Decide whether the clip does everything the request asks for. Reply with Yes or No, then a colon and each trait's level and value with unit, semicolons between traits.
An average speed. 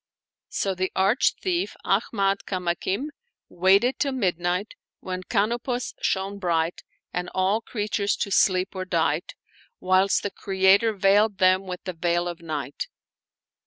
No: slow, 130 wpm